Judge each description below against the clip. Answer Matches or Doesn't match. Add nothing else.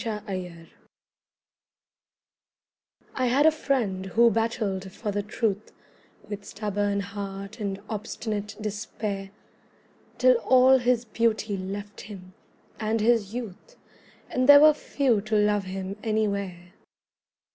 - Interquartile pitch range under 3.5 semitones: Matches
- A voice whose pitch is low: Doesn't match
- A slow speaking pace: Matches